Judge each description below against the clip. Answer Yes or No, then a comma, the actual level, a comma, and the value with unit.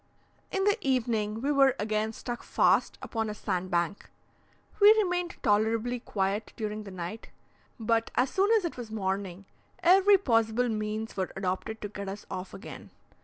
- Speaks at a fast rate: No, average, 160 wpm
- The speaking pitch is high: Yes, high, 220 Hz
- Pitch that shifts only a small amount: No, average, 4.2 semitones